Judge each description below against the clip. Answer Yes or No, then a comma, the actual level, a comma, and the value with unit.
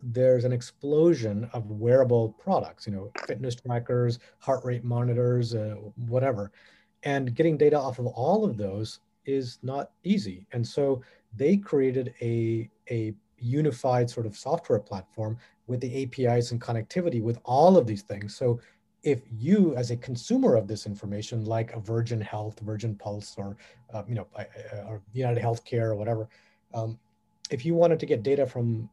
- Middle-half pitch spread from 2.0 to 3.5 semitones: Yes, average, 3.2 semitones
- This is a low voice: Yes, low, 120 Hz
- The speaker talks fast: No, average, 165 wpm